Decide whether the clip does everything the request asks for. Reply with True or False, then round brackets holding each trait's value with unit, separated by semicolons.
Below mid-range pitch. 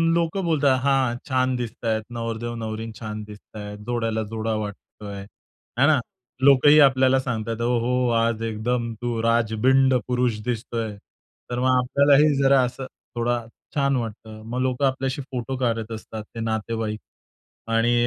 True (120 Hz)